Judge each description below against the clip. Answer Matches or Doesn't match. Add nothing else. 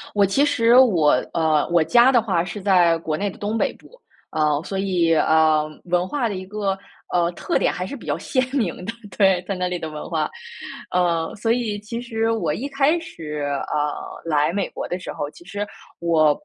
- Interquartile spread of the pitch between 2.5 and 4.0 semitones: Doesn't match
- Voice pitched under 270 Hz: Matches